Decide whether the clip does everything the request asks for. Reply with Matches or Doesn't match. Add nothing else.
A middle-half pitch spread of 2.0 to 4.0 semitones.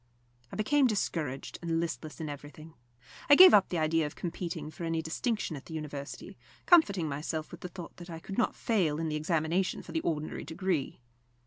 Matches